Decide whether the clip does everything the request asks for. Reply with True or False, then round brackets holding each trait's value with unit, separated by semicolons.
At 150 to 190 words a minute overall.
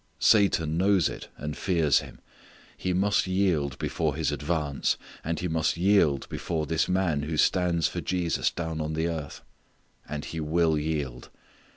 True (160 wpm)